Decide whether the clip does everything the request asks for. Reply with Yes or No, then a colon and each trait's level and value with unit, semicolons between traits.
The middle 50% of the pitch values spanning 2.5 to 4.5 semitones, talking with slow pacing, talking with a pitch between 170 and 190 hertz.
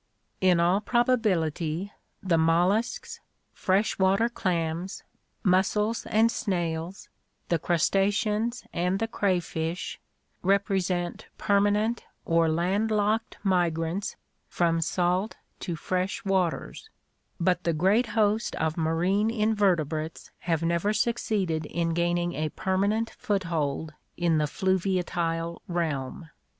Yes: average, 3.6 semitones; slow, 110 wpm; medium, 185 Hz